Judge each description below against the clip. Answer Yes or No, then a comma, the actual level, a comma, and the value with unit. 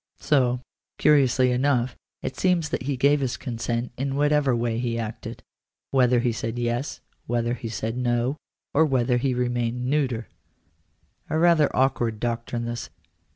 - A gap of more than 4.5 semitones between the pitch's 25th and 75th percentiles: No, narrow, 2.6 semitones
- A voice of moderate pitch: No, low, 125 Hz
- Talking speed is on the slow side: No, average, 155 wpm